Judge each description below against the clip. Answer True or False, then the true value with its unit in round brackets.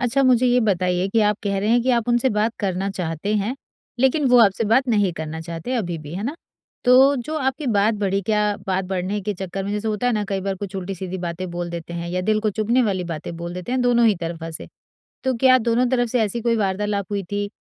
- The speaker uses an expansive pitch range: False (4.4 semitones)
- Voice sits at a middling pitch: False (205 Hz)